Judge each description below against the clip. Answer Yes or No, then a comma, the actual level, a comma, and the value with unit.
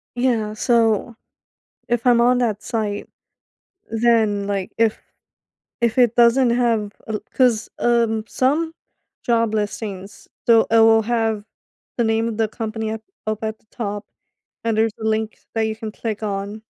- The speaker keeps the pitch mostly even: Yes, narrow, 1.6 semitones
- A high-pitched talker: Yes, high, 225 Hz